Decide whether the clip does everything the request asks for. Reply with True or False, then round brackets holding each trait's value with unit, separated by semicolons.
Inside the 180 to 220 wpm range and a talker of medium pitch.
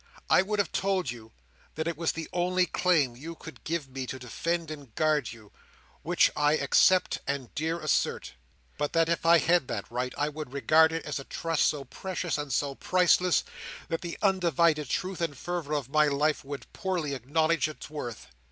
True (200 wpm; 155 Hz)